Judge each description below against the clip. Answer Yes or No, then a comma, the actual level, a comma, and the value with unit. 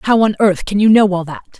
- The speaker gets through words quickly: Yes, fast, 300 wpm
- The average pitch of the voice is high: Yes, high, 200 Hz